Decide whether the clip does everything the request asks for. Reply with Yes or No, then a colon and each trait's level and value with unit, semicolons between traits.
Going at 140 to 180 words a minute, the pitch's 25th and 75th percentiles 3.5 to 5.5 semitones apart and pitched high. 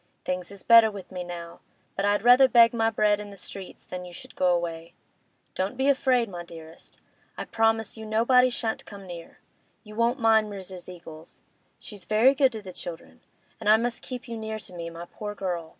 No: fast, 205 wpm; average, 4.3 semitones; high, 205 Hz